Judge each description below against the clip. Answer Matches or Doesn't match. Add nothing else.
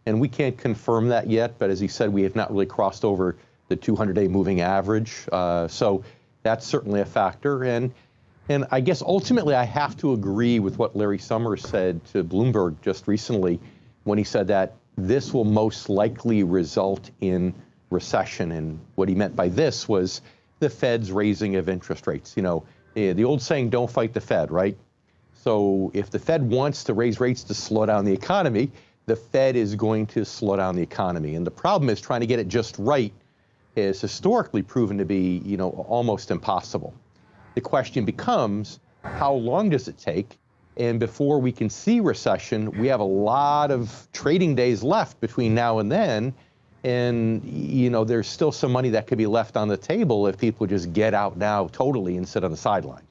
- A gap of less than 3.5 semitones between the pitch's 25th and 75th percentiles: Doesn't match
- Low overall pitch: Matches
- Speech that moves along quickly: Doesn't match